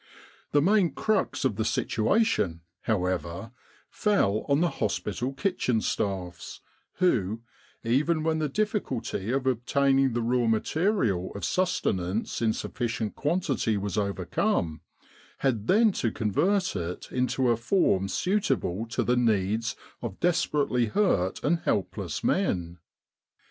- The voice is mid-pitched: No, low, 120 Hz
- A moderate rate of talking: No, slow, 125 wpm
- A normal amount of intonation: No, wide, 7.9 semitones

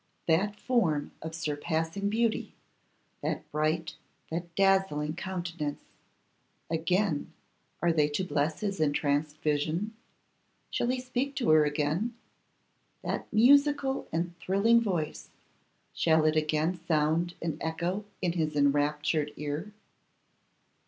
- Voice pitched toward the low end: No, medium, 165 Hz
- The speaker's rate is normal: No, slow, 110 wpm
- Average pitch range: Yes, average, 4.5 semitones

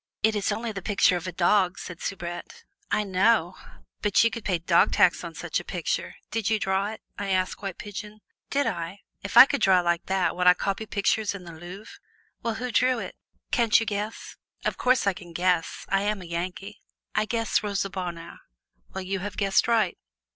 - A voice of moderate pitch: No, high, 200 Hz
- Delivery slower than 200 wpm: No, fast, 205 wpm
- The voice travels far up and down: No, average, 3.1 semitones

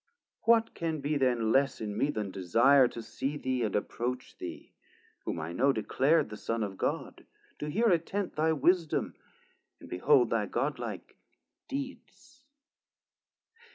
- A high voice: No, medium, 140 Hz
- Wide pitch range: Yes, wide, 6.4 semitones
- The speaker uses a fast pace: No, average, 150 wpm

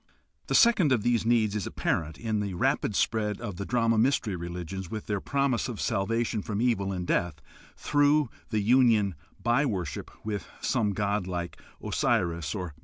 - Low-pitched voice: Yes, low, 105 Hz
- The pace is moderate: Yes, average, 175 wpm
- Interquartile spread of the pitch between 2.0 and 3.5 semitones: No, average, 4.1 semitones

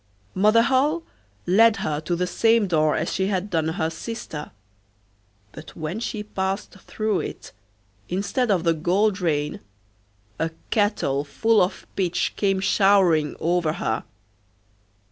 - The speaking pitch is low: No, high, 190 Hz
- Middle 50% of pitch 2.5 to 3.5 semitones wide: No, average, 4.6 semitones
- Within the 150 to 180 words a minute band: No, slow, 135 wpm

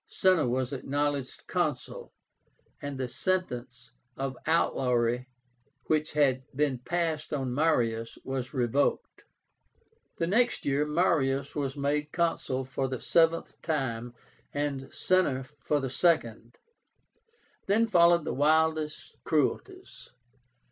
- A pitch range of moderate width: Yes, average, 3.7 semitones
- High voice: No, medium, 145 Hz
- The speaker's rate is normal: No, slow, 110 wpm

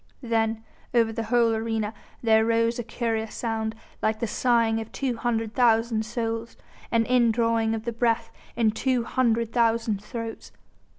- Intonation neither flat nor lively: No, narrow, 0.9 semitones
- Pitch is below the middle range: No, high, 230 Hz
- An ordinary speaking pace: Yes, average, 155 wpm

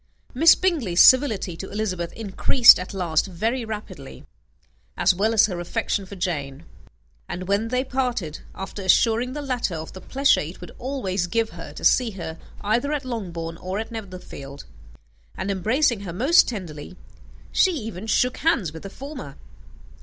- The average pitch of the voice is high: Yes, high, 205 Hz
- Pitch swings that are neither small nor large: No, wide, 5.9 semitones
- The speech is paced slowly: No, average, 160 wpm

